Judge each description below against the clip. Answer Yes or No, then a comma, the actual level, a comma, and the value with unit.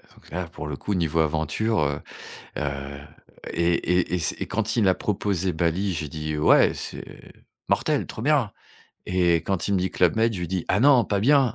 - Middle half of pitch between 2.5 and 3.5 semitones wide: No, average, 4.6 semitones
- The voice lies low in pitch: Yes, very low, 90 Hz